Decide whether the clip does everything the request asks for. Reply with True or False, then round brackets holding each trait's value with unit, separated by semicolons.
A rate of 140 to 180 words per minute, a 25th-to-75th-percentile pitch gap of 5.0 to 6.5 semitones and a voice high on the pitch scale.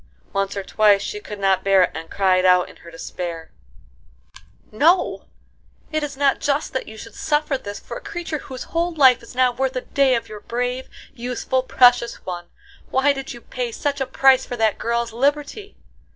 False (195 wpm; 5.5 semitones; 250 Hz)